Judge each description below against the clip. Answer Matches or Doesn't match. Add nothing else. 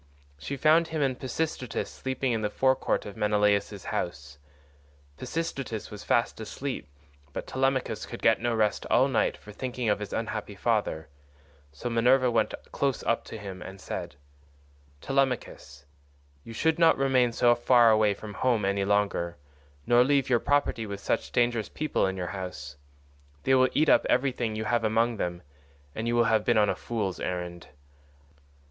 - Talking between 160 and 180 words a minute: Matches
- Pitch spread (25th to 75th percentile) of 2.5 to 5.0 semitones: Matches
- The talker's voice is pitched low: Matches